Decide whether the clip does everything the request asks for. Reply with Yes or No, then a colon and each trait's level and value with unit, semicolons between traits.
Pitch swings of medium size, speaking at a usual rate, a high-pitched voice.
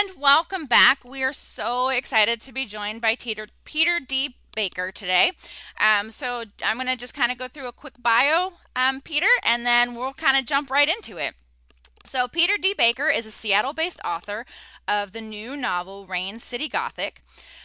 Yes: average, 5.0 semitones; average, 180 wpm; very high, 255 Hz